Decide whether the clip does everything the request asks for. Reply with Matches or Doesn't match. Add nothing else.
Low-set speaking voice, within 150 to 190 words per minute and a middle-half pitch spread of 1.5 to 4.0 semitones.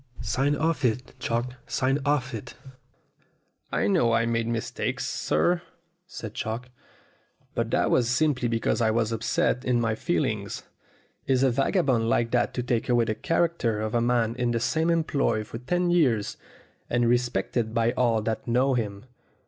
Matches